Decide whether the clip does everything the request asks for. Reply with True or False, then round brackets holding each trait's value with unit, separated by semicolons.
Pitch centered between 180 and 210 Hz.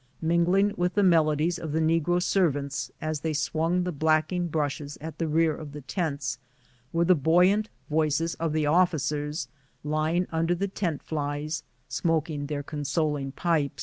False (160 Hz)